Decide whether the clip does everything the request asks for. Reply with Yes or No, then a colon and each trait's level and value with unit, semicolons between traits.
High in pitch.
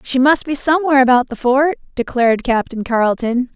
Yes: very high, 260 Hz